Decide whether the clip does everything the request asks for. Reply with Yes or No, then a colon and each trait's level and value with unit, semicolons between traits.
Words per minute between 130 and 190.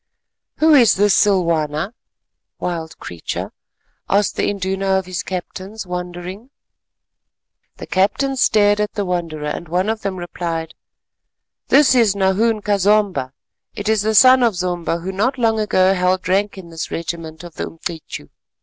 Yes: average, 150 wpm